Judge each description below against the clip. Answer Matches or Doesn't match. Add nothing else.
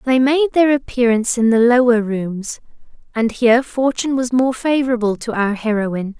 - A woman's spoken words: Matches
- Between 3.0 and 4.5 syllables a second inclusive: Doesn't match